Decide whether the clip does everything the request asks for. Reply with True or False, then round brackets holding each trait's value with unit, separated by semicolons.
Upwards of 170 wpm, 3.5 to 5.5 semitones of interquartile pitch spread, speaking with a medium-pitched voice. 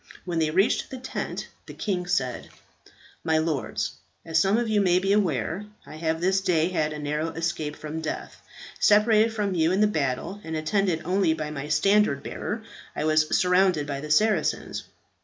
True (180 wpm; 4.2 semitones; 165 Hz)